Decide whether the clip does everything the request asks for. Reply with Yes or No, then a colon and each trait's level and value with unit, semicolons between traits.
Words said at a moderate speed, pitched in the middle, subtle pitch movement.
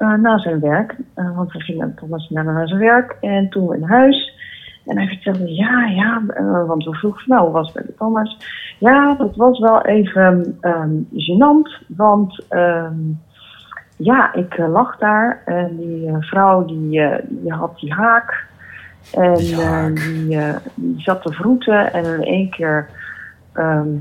No: average, 160 wpm; medium, 180 Hz; average, 5.0 semitones